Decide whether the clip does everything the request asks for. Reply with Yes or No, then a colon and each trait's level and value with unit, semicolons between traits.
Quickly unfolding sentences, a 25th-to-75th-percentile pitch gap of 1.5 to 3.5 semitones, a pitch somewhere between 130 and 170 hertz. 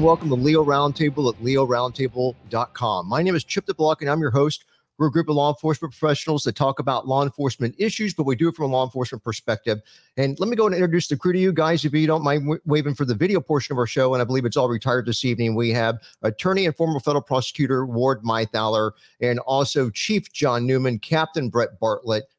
No: fast, 230 wpm; average, 4.0 semitones; medium, 140 Hz